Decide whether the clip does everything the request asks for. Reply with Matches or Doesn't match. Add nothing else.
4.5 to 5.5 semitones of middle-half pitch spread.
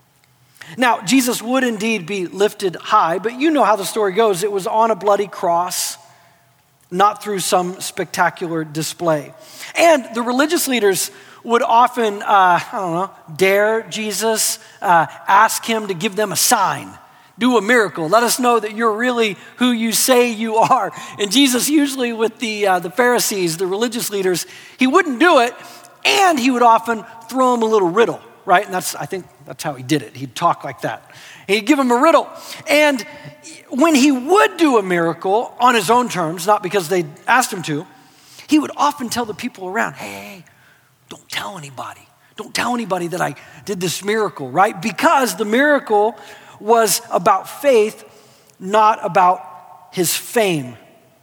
Matches